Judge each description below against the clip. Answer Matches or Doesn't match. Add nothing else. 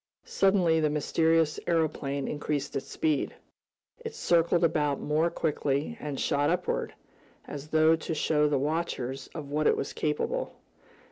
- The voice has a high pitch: Doesn't match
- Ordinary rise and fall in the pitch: Doesn't match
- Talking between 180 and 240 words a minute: Doesn't match